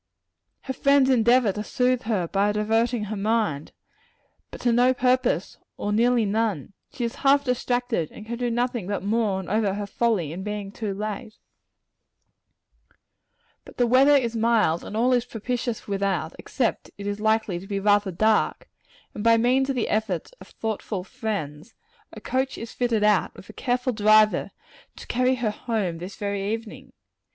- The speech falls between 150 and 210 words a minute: Yes, average, 170 wpm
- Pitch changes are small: No, average, 3.3 semitones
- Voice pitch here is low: No, high, 220 Hz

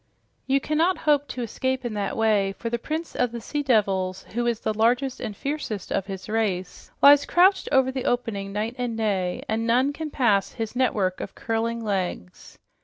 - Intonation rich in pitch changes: No, average, 4.4 semitones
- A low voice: No, high, 230 Hz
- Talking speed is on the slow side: No, average, 190 wpm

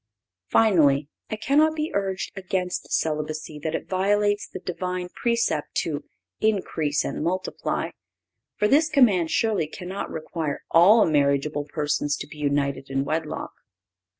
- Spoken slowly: Yes, slow, 130 wpm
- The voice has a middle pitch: Yes, medium, 175 Hz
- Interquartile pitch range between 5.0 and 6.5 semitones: Yes, wide, 5.5 semitones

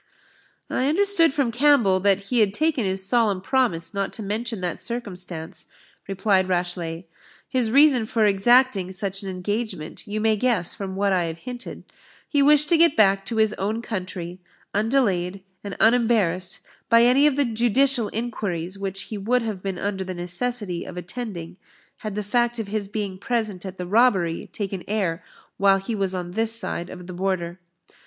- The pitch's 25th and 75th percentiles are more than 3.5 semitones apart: Yes, average, 4.2 semitones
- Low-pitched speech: No, high, 205 Hz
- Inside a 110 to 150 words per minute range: No, average, 175 wpm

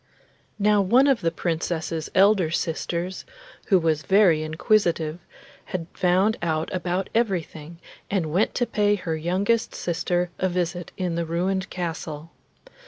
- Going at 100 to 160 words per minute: Yes, slow, 135 wpm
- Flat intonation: No, average, 3.0 semitones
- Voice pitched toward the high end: No, medium, 175 Hz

